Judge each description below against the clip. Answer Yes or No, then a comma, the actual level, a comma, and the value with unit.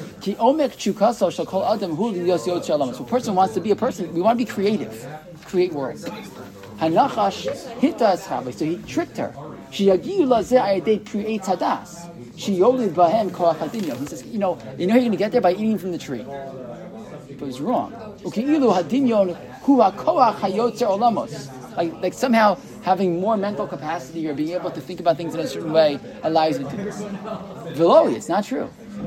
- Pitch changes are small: No, average, 4.5 semitones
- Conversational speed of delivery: No, slow, 125 wpm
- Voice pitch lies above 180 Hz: Yes, high, 190 Hz